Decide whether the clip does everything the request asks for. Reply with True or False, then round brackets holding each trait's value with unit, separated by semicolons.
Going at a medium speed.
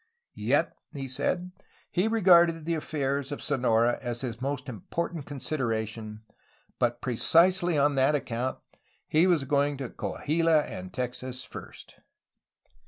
False (130 wpm)